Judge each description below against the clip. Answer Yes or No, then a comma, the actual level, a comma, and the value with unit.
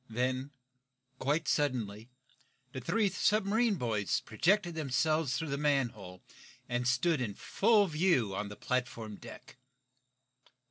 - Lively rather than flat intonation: Yes, wide, 6.1 semitones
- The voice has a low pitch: Yes, low, 130 Hz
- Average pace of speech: No, slow, 120 wpm